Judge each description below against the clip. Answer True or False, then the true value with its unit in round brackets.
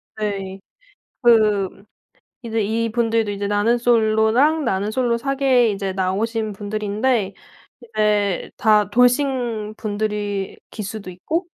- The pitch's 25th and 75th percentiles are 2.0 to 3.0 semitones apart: True (2.5 semitones)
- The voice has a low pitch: False (215 Hz)